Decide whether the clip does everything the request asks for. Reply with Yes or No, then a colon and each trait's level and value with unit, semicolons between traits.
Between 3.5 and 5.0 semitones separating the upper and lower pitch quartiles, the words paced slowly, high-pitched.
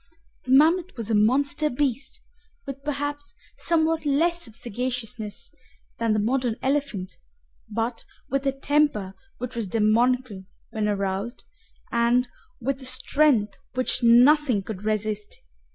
Yes: average, 4.6 semitones; slow, 125 wpm; high, 245 Hz